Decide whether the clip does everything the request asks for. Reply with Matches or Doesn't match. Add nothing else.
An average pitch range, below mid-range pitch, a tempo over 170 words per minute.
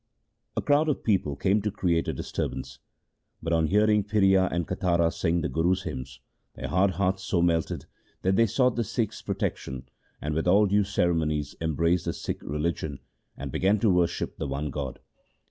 Matches